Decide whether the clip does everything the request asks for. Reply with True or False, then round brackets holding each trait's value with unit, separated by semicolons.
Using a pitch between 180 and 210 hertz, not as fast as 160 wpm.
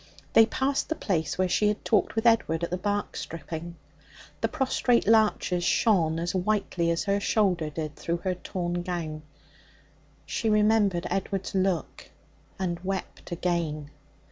True (185 Hz; 145 wpm)